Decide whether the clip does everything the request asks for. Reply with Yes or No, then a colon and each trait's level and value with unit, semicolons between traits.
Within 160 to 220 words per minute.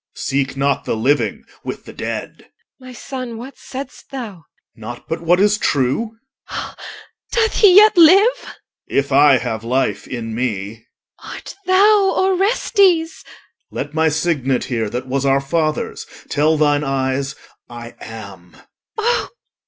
No: average, 150 wpm